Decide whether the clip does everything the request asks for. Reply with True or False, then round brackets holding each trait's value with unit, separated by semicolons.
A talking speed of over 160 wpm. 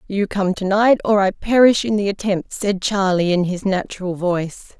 True (200 wpm)